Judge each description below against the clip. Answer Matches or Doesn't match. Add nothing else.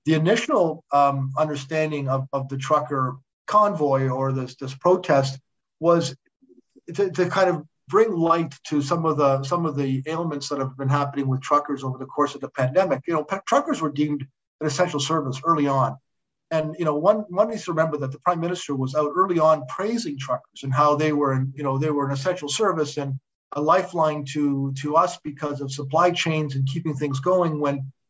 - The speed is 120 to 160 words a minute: Doesn't match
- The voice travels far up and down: Doesn't match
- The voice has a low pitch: Doesn't match